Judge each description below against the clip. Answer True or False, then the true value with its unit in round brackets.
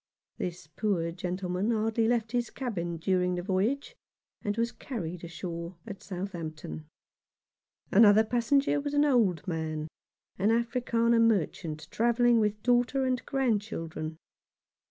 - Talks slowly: True (125 wpm)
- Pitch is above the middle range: True (205 Hz)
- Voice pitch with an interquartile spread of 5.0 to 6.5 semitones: True (5.4 semitones)